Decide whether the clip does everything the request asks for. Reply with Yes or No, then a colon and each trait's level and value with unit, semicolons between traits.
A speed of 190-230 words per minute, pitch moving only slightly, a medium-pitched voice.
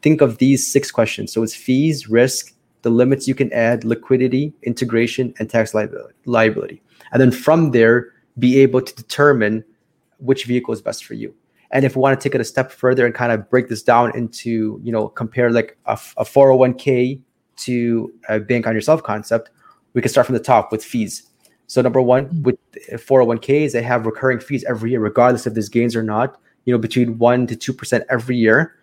No: average, 200 wpm; narrow, 2.3 semitones; low, 125 Hz